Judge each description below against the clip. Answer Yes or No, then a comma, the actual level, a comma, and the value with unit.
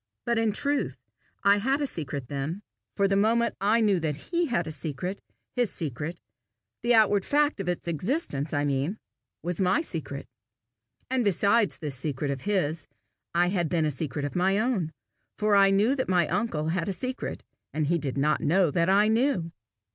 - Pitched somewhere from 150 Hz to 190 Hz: Yes, medium, 185 Hz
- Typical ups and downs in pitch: No, wide, 6.0 semitones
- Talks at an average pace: Yes, average, 185 wpm